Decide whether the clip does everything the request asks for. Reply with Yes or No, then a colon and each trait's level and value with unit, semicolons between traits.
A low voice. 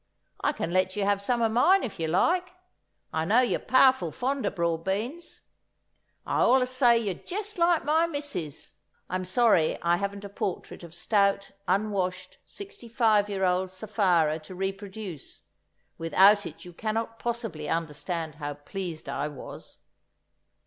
No: high, 200 Hz